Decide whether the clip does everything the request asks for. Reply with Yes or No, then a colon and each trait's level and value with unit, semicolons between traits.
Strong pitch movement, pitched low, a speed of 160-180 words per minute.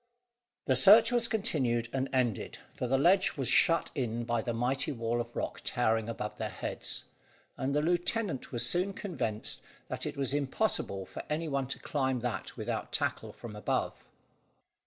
Yes: wide, 5.8 semitones; low, 130 Hz; average, 170 wpm